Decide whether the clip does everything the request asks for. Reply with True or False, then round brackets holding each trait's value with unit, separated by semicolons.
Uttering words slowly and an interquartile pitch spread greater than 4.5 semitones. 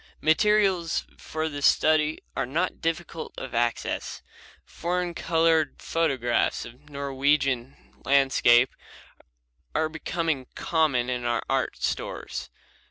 False (100 wpm; 3.8 semitones)